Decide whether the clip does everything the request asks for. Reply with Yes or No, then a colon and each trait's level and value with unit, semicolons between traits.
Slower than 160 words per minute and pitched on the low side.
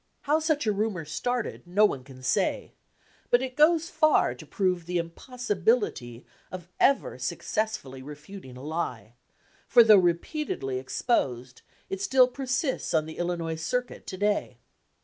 No: average, 150 wpm; high, 190 Hz